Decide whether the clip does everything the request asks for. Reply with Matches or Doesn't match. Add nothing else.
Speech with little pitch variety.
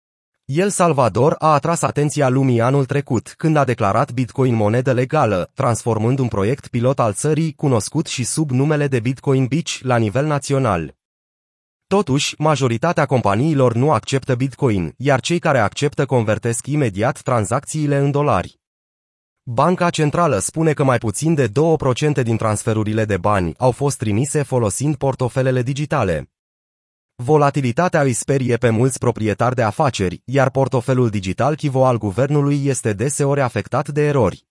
Doesn't match